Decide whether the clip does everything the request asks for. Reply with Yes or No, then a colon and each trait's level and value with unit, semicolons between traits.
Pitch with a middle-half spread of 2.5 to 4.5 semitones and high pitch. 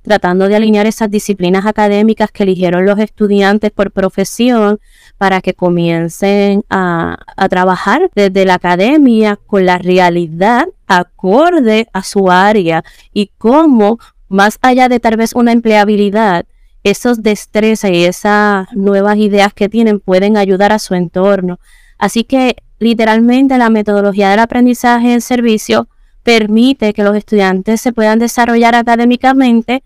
Yes: average, 2.9 semitones; high, 210 Hz